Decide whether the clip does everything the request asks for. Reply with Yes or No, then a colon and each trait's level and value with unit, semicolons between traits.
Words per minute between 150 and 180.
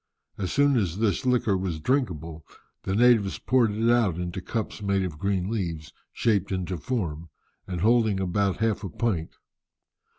Yes: average, 160 wpm